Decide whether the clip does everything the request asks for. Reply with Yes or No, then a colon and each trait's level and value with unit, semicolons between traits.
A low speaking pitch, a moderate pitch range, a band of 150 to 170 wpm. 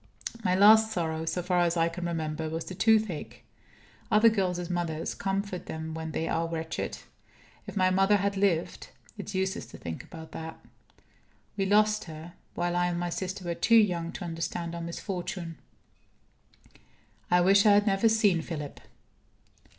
No: medium, 175 Hz; average, 3.1 semitones; average, 165 wpm